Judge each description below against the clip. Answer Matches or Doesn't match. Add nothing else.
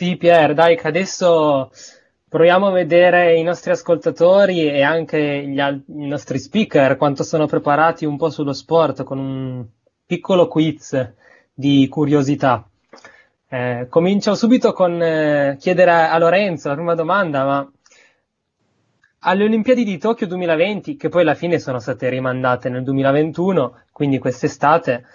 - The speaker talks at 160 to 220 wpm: Doesn't match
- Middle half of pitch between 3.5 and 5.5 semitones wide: Matches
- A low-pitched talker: Doesn't match